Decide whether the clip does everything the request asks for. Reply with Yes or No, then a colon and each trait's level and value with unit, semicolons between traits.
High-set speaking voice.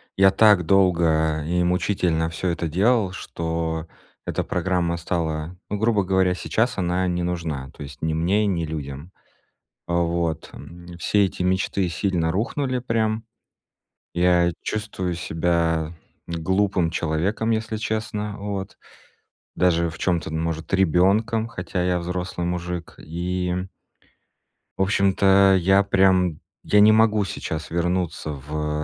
No: very low, 90 Hz